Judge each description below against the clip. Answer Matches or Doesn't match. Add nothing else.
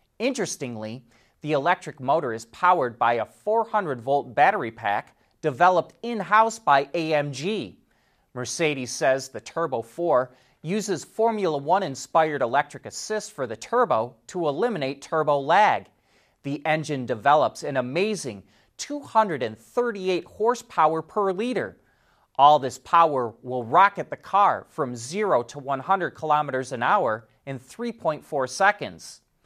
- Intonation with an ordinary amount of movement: Doesn't match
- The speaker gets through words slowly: Matches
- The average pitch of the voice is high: Doesn't match